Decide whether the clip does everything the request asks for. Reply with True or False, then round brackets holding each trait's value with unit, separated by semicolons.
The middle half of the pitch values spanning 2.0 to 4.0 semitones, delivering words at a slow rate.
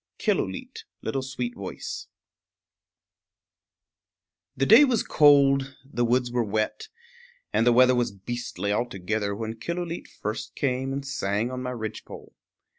True (3.7 semitones; 115 wpm)